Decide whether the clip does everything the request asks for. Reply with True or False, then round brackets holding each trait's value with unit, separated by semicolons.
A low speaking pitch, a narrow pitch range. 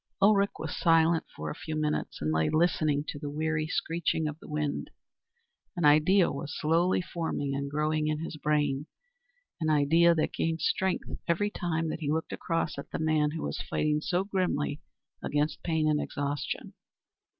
False (155 Hz; 2.0 semitones)